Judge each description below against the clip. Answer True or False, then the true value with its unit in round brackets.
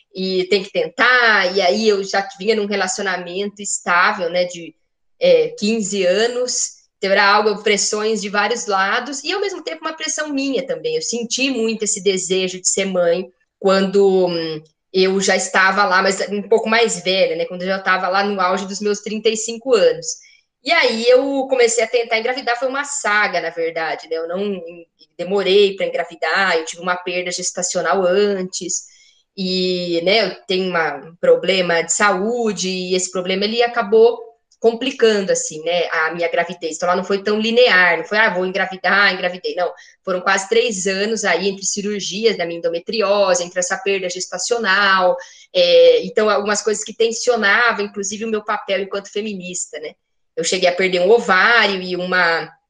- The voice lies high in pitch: True (200 Hz)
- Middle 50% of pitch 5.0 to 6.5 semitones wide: False (3.9 semitones)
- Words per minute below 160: False (175 wpm)